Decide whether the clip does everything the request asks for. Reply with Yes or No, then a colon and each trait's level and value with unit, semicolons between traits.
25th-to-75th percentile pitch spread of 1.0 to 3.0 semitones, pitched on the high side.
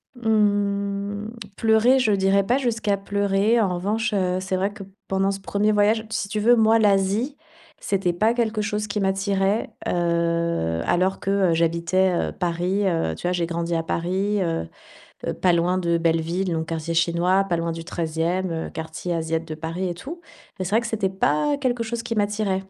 No: average, 3.7 semitones; high, 195 Hz